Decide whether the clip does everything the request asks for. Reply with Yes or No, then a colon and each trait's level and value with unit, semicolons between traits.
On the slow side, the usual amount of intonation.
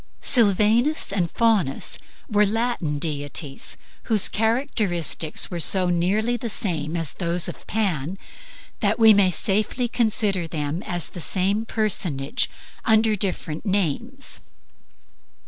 Yes: slow, 115 wpm; average, 4.7 semitones